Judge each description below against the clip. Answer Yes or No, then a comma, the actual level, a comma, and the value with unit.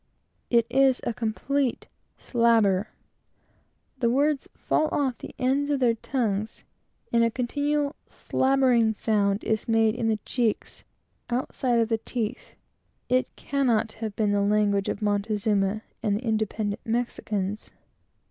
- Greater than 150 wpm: No, slow, 135 wpm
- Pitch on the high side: Yes, high, 230 Hz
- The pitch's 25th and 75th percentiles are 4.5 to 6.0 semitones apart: No, average, 3.2 semitones